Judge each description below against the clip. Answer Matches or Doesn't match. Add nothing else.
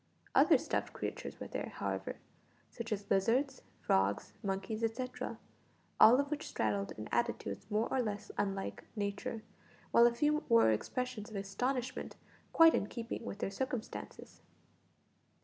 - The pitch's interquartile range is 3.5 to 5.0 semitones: Matches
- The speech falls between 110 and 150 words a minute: Matches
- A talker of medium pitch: Doesn't match